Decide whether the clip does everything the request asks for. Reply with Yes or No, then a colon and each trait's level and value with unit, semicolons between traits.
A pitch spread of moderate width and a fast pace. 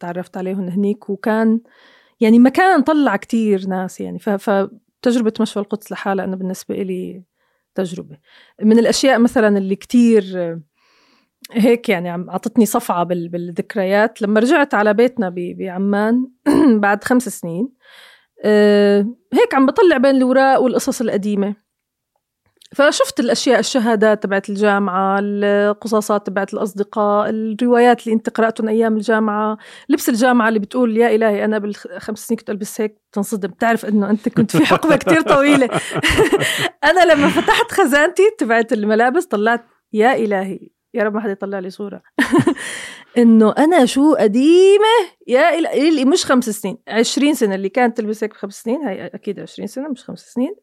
Yes: average, 4.0 semitones; fast, 140 wpm